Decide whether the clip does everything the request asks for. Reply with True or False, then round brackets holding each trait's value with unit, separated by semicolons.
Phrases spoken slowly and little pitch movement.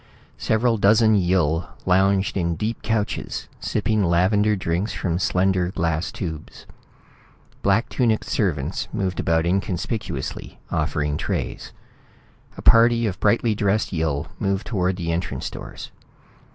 False (120 wpm; 3.9 semitones)